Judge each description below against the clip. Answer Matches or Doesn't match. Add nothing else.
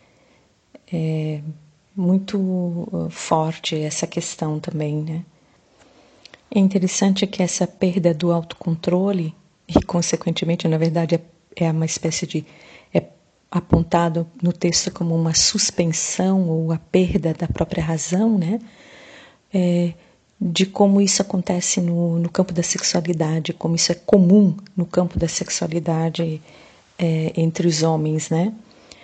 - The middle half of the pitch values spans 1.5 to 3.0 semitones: Matches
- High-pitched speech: Doesn't match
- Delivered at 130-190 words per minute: Doesn't match